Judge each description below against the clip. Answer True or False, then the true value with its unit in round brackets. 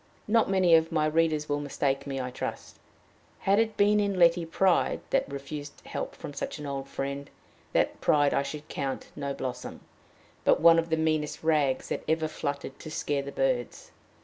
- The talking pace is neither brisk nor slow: True (185 wpm)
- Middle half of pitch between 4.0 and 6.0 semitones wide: False (2.9 semitones)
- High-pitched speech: False (150 Hz)